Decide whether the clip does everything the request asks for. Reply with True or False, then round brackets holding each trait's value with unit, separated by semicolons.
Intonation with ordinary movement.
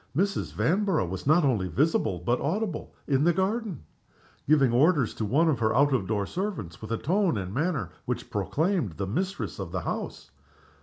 False (8.7 semitones)